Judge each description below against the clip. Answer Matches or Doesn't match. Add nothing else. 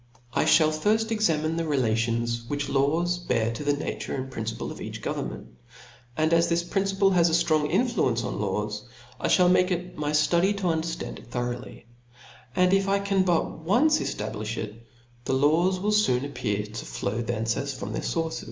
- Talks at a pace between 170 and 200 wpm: Matches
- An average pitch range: Doesn't match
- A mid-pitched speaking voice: Matches